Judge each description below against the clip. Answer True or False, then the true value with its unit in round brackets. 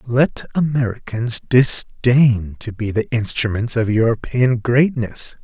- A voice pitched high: False (120 Hz)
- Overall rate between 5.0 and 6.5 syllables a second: False (3.7 syllables/s)